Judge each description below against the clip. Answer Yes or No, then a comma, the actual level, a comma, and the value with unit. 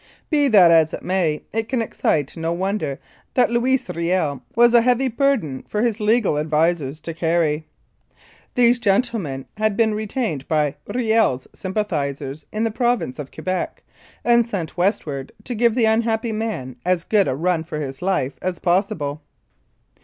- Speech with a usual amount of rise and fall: No, wide, 6.7 semitones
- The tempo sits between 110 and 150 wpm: No, average, 160 wpm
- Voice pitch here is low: No, medium, 185 Hz